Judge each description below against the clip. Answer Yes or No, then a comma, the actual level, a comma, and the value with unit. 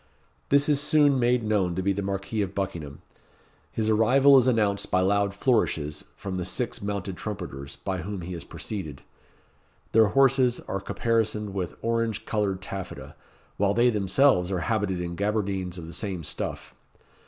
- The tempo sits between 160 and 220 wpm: Yes, average, 165 wpm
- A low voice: Yes, low, 100 Hz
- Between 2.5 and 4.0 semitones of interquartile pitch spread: Yes, average, 3.6 semitones